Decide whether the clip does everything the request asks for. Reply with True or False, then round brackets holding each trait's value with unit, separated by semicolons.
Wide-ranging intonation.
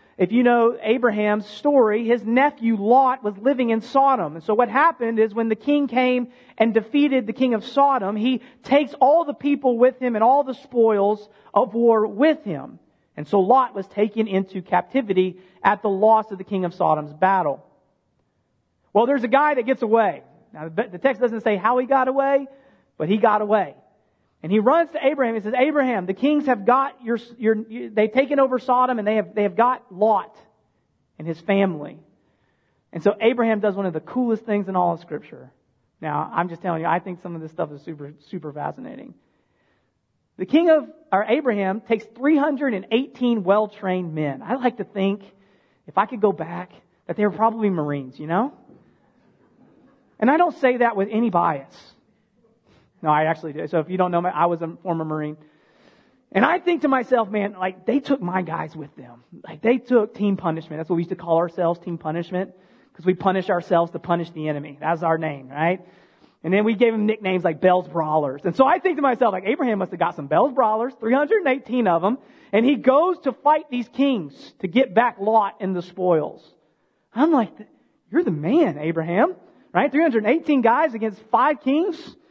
True (5.9 semitones)